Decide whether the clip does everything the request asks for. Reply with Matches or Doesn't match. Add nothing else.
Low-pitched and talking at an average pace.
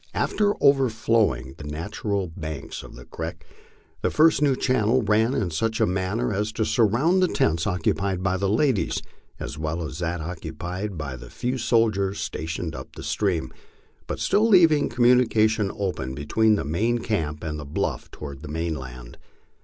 Matches